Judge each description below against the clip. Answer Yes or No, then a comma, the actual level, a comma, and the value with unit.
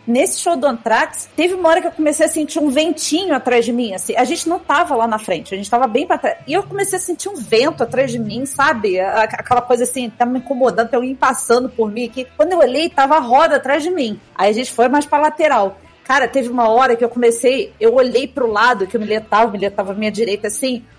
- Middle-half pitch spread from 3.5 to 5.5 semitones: Yes, average, 5.0 semitones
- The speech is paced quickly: Yes, fast, 265 wpm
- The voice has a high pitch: Yes, very high, 260 Hz